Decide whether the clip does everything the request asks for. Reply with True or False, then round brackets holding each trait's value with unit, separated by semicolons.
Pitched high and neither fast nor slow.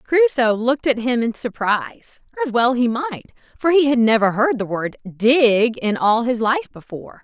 True (245 Hz; 190 wpm)